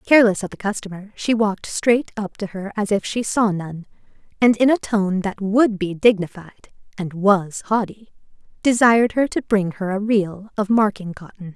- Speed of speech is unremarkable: Yes, average, 185 wpm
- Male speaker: No, female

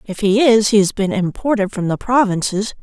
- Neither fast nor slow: No, fast, 215 wpm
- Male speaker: No, female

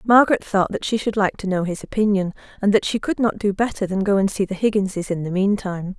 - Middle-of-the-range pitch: No, high, 200 Hz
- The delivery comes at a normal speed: No, fast, 260 wpm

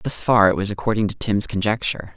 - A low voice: Yes, low, 105 Hz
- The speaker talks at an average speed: No, fast, 220 wpm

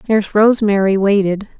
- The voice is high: Yes, high, 205 Hz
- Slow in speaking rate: Yes, slow, 115 wpm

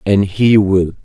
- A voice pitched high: No, low, 100 Hz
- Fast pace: No, average, 175 wpm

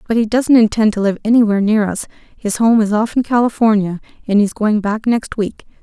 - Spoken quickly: Yes, fast, 215 wpm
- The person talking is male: No, female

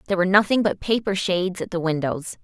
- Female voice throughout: Yes, female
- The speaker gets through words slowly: No, fast, 220 wpm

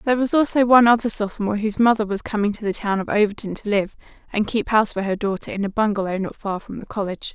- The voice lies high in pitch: Yes, high, 210 Hz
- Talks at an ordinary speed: No, fast, 255 wpm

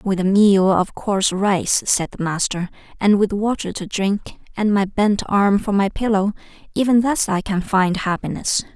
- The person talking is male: No, female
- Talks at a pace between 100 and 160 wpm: No, average, 180 wpm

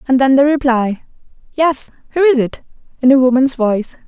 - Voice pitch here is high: Yes, very high, 260 Hz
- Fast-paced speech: No, average, 175 wpm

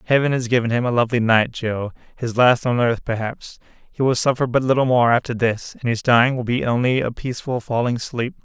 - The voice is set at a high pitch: No, low, 120 Hz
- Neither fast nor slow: No, fast, 215 wpm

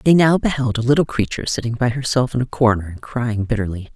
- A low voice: Yes, low, 120 Hz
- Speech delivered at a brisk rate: Yes, fast, 230 wpm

